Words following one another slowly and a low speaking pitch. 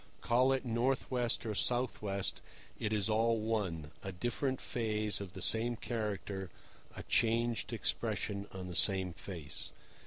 No: average, 145 wpm; low, 110 Hz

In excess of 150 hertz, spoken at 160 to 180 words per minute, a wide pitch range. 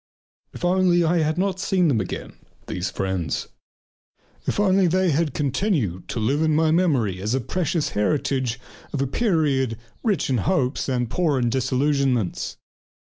No: medium, 140 Hz; average, 170 wpm; wide, 6.3 semitones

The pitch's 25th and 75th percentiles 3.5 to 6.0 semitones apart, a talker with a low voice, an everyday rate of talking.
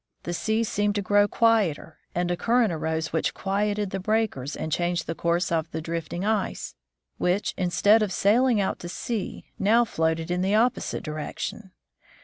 No: average, 4.1 semitones; high, 190 Hz; average, 170 wpm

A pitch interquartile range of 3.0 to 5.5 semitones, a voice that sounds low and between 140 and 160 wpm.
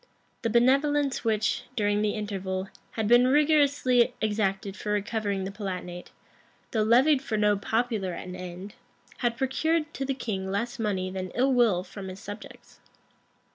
No: average, 4.3 semitones; high, 215 Hz; average, 150 wpm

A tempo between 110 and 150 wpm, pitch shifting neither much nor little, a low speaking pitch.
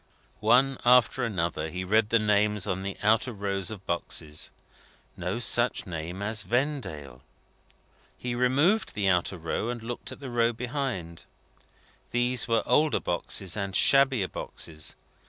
Yes: average, 140 wpm; average, 4.9 semitones; low, 105 Hz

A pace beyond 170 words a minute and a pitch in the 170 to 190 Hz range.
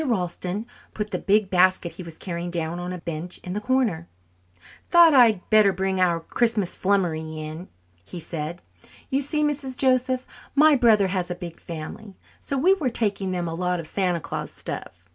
Yes: average, 180 wpm; medium, 185 Hz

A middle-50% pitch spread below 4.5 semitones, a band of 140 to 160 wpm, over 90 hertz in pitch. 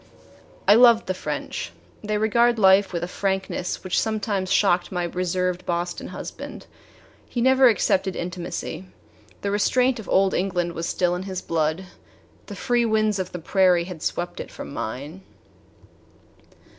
Yes: average, 3.2 semitones; average, 150 wpm; high, 190 Hz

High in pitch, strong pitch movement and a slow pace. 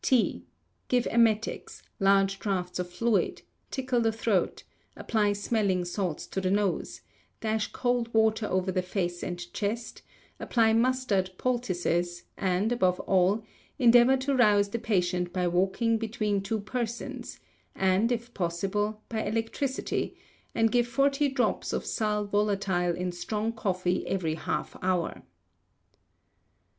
No: high, 210 Hz; average, 3.9 semitones; slow, 130 wpm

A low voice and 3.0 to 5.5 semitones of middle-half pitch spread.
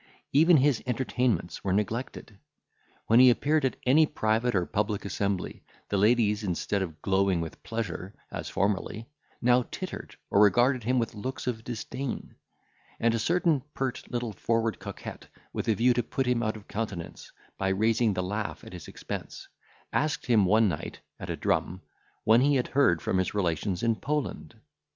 Yes: low, 110 Hz; average, 4.0 semitones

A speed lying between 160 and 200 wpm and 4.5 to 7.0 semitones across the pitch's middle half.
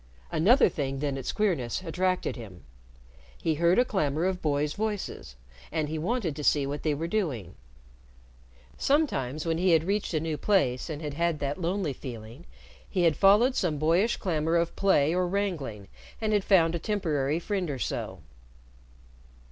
Yes: average, 170 wpm; average, 4.8 semitones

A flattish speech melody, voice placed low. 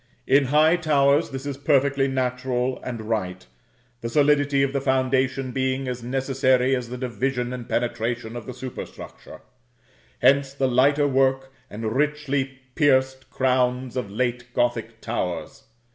Yes: narrow, 1.9 semitones; low, 130 Hz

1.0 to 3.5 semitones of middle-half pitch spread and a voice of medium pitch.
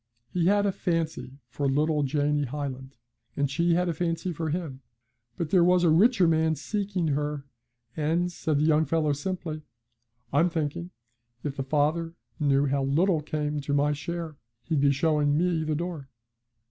Yes: average, 2.9 semitones; medium, 155 Hz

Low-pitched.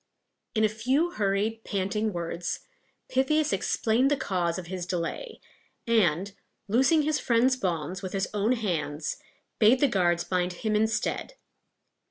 No: high, 210 Hz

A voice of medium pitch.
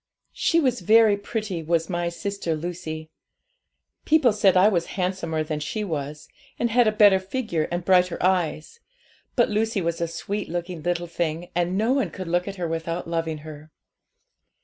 Yes: medium, 175 Hz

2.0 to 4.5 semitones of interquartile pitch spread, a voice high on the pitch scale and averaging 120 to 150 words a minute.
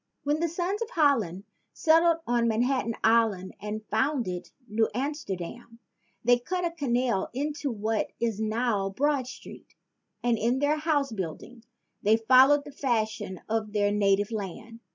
No: average, 5.0 semitones; high, 235 Hz; average, 145 wpm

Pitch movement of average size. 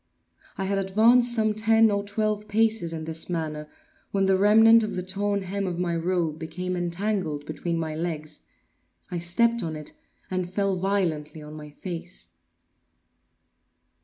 Yes: average, 4.0 semitones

